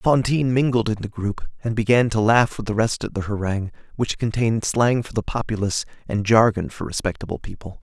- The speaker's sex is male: Yes, male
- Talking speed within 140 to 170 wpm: No, average, 200 wpm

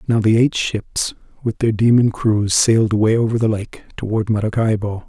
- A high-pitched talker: No, low, 110 Hz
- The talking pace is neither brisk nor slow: Yes, average, 175 wpm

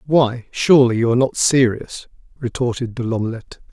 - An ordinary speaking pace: Yes, average, 145 wpm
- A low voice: Yes, low, 120 Hz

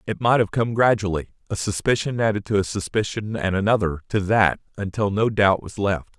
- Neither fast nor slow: Yes, average, 195 wpm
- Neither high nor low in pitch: No, low, 105 Hz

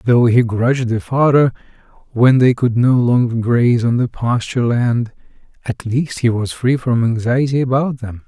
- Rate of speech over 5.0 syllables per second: No, 4.7 syllables/s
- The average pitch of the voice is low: Yes, low, 120 Hz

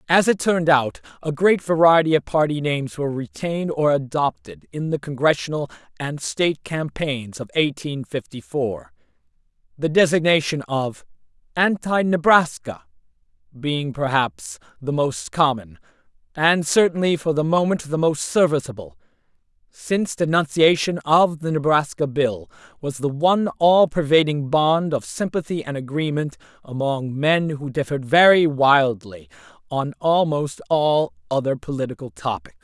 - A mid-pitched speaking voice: Yes, medium, 150 Hz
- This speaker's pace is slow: Yes, slow, 130 wpm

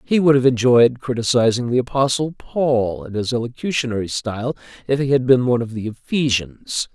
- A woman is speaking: No, male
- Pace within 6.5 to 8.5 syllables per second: No, 5.4 syllables/s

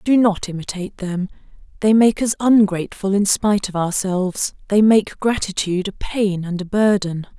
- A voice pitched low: No, high, 200 Hz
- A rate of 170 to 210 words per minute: No, average, 160 wpm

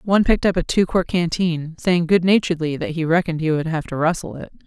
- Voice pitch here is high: No, medium, 165 Hz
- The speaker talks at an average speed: No, fast, 245 wpm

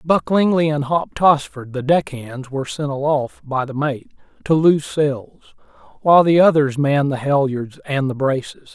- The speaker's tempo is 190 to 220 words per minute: No, average, 180 wpm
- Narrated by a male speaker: Yes, male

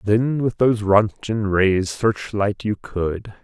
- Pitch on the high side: No, low, 105 Hz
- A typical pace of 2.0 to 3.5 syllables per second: Yes, 3.4 syllables/s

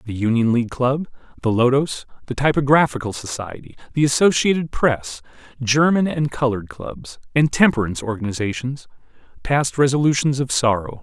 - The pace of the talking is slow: Yes, slow, 125 wpm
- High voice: No, low, 130 Hz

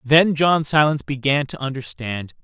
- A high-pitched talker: No, low, 135 Hz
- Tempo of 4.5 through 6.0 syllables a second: Yes, 4.8 syllables/s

